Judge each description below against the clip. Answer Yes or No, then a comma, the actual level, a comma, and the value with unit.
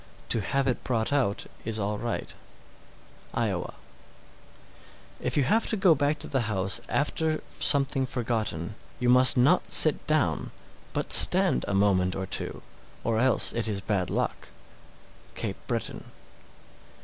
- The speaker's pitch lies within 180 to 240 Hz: No, low, 120 Hz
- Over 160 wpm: No, average, 145 wpm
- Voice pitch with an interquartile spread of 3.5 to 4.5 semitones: No, average, 5.2 semitones